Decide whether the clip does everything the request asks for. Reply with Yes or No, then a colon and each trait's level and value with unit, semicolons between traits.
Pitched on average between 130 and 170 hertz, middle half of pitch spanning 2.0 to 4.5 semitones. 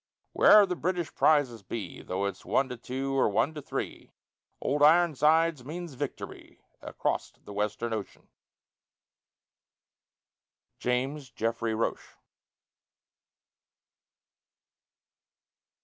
No: low, 135 Hz; wide, 5.4 semitones